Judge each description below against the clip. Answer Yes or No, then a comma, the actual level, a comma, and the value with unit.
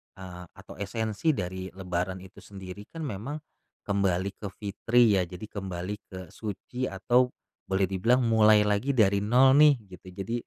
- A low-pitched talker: Yes, low, 100 Hz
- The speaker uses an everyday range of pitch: Yes, average, 3.6 semitones